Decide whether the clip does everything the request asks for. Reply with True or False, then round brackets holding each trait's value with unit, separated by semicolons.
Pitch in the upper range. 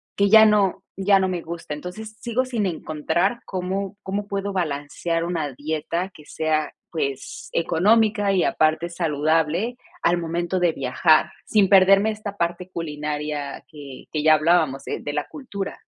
False (175 Hz)